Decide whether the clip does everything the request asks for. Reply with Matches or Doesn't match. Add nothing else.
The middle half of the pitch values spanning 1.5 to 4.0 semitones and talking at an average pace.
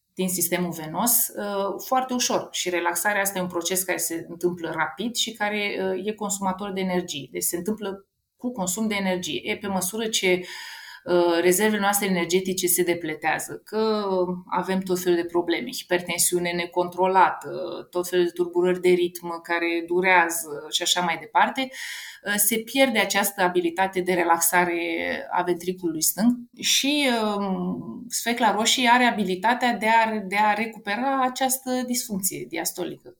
Matches